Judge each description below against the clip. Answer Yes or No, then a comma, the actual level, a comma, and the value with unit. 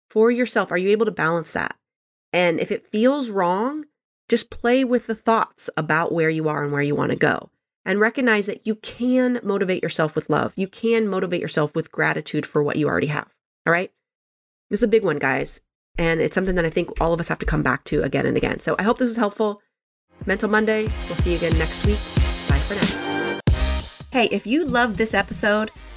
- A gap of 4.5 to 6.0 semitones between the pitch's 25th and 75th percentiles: Yes, wide, 5.5 semitones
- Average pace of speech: No, fast, 220 wpm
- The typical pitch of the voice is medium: No, high, 210 Hz